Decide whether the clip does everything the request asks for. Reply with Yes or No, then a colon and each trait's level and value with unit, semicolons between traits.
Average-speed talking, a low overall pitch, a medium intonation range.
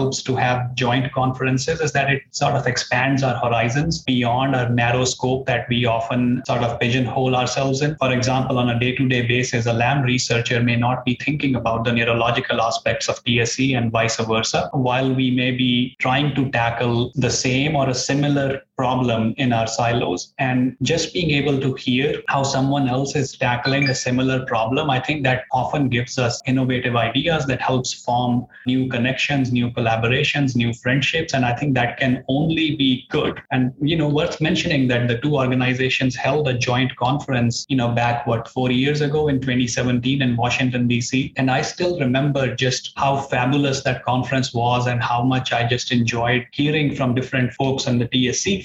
No: average, 185 wpm; low, 130 Hz; narrow, 1.9 semitones